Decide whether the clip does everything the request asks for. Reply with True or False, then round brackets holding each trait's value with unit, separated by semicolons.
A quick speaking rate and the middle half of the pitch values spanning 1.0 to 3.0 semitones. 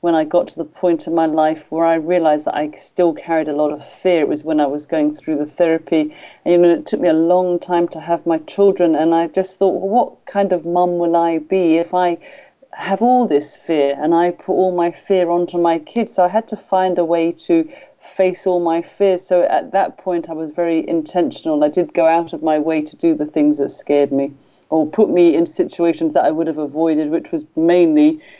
True (245 wpm; 2.4 semitones)